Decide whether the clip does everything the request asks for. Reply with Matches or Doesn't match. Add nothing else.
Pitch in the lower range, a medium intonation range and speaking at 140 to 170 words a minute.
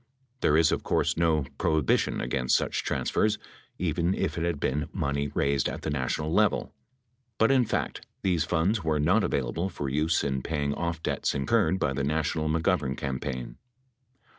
Matches